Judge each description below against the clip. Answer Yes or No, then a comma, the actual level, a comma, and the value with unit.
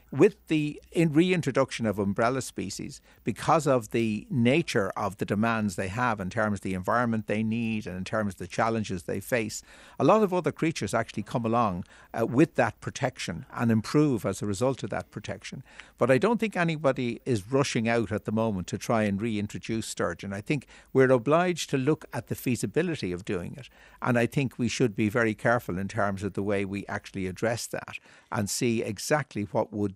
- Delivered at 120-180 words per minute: No, average, 200 wpm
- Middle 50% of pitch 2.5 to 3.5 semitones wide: No, average, 4.3 semitones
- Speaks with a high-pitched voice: No, low, 115 Hz